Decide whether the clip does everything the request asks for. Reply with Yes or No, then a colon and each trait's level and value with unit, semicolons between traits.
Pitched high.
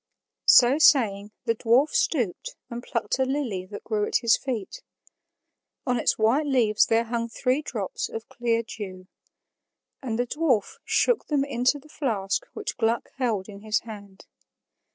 Yes: high, 235 Hz